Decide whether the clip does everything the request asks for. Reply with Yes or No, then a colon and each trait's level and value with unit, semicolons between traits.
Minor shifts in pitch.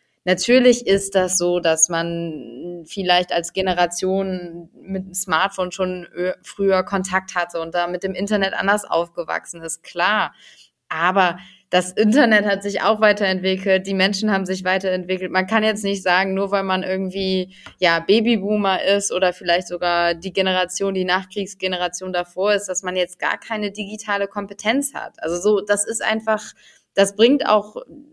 Yes: narrow, 2.0 semitones